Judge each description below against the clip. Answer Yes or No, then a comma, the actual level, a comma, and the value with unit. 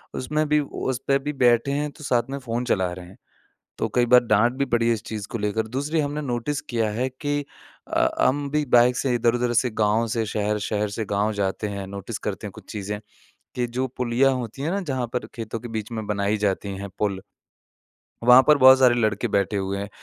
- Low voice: Yes, low, 120 Hz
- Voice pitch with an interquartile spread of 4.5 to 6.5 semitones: No, average, 4.0 semitones